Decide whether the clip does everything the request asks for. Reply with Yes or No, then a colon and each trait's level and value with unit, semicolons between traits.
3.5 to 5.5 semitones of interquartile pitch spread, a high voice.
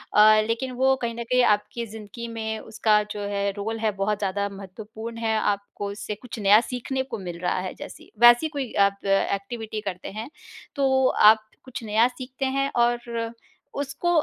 No: average, 2.9 semitones; high, 220 Hz